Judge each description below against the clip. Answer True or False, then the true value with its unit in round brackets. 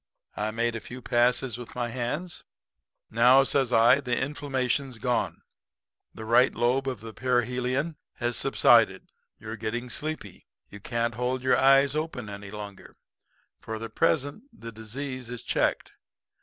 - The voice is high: False (125 Hz)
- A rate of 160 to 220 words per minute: False (145 wpm)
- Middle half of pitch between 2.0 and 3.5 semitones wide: True (2.7 semitones)